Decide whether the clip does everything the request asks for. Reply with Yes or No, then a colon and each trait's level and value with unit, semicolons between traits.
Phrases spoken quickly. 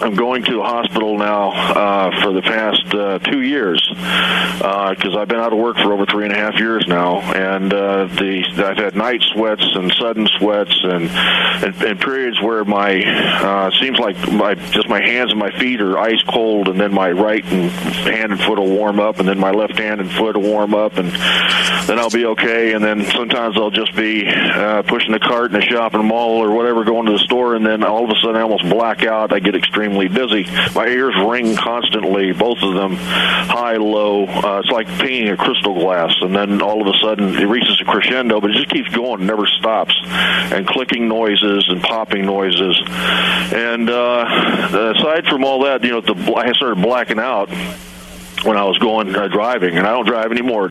Yes: fast, 210 wpm